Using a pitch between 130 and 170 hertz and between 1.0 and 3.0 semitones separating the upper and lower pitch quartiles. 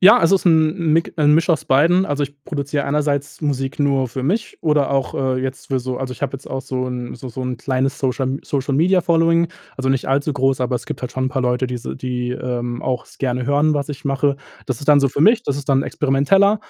Yes: medium, 140 Hz; narrow, 2.6 semitones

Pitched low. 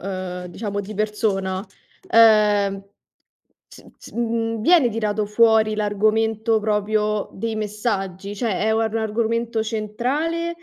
No: high, 215 Hz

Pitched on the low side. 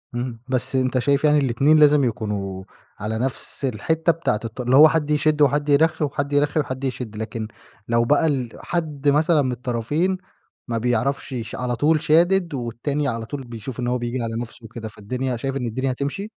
Yes: low, 130 Hz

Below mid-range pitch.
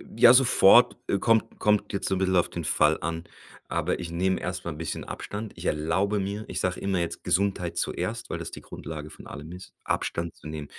Yes: very low, 90 Hz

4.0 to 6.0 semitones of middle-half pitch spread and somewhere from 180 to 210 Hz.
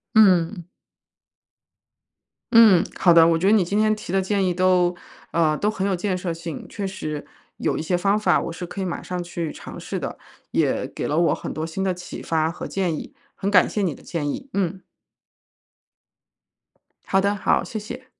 No: average, 3.0 semitones; medium, 185 Hz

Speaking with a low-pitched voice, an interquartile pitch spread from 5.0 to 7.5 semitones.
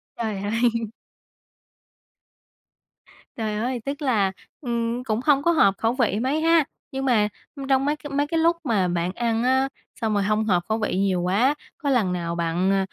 No: high, 230 Hz; wide, 5.4 semitones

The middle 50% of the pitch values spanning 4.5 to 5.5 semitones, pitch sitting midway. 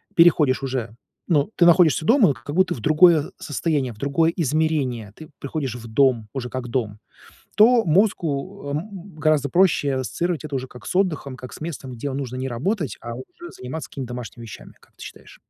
Yes: average, 4.8 semitones; medium, 145 Hz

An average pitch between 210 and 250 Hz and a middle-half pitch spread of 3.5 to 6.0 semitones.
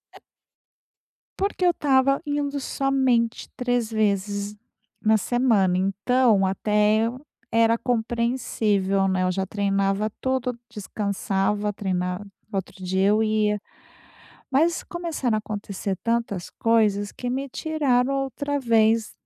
Yes: high, 220 Hz; average, 4.1 semitones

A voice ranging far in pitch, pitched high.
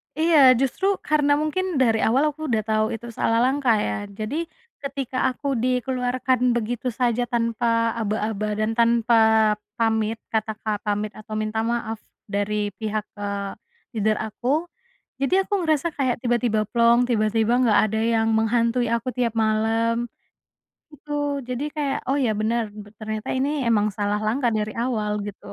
No: average, 2.8 semitones; high, 230 Hz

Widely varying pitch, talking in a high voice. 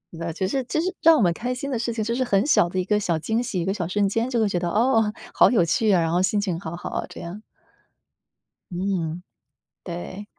No: average, 4.7 semitones; high, 200 Hz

